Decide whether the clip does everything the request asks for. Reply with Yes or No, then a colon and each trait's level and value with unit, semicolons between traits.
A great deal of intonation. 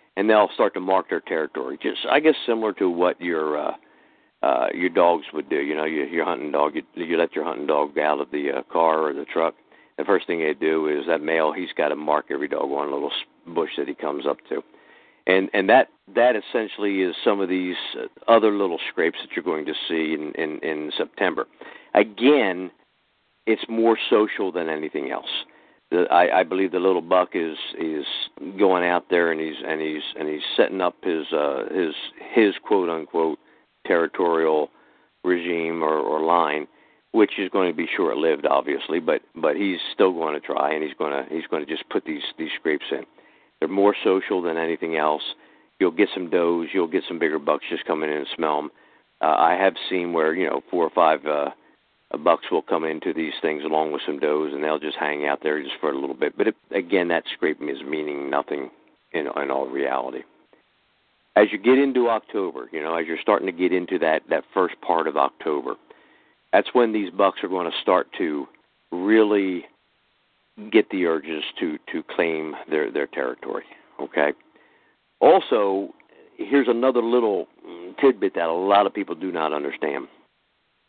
No: average, 3.8 semitones